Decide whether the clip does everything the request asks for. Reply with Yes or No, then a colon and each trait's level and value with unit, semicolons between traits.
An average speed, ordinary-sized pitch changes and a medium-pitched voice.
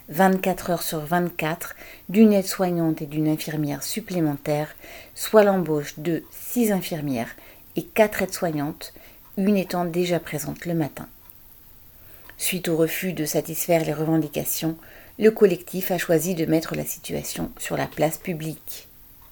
No: slow, 135 wpm; average, 3.3 semitones; medium, 165 Hz